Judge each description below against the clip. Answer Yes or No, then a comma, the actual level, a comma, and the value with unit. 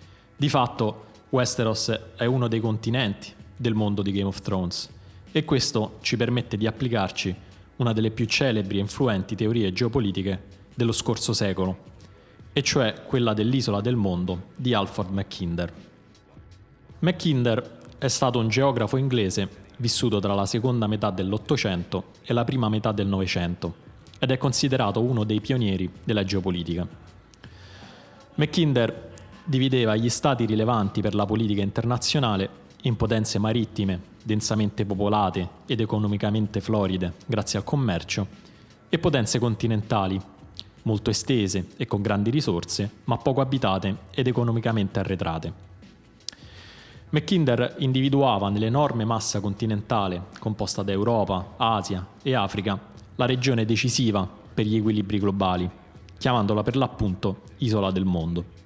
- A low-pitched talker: Yes, low, 110 Hz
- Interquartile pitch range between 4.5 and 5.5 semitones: No, average, 3.6 semitones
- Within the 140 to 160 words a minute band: No, average, 125 wpm